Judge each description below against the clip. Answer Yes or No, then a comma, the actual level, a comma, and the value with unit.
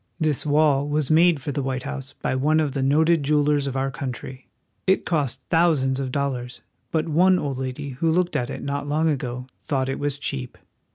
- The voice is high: No, medium, 145 Hz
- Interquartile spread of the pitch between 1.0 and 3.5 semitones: Yes, narrow, 2.6 semitones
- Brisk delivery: Yes, fast, 210 wpm